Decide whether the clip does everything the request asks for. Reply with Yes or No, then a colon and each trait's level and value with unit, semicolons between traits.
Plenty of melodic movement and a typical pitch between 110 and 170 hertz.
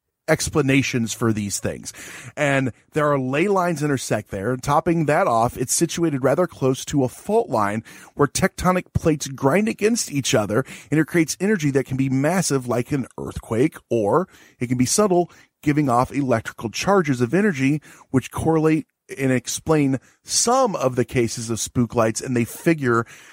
No: average, 4.7 semitones; low, 135 Hz